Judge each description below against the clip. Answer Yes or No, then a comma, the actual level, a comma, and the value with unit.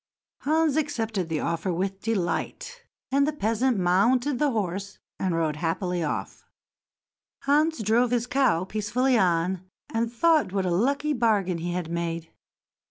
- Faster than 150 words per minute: No, average, 145 wpm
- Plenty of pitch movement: Yes, wide, 6.8 semitones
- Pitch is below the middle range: No, high, 210 Hz